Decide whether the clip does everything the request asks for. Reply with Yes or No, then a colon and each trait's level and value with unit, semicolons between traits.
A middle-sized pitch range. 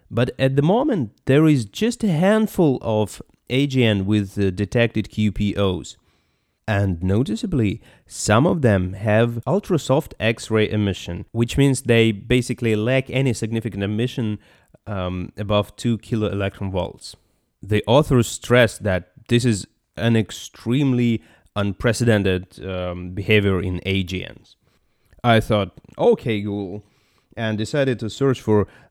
Yes: average, 3.7 semitones